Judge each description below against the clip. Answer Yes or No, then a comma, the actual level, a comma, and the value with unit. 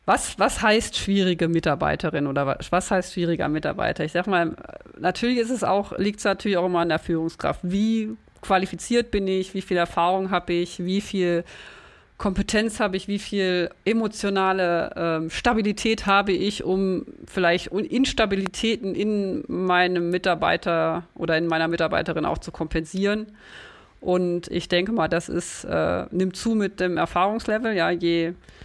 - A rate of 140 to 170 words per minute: Yes, average, 155 wpm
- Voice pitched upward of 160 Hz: Yes, medium, 185 Hz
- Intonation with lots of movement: No, average, 3.0 semitones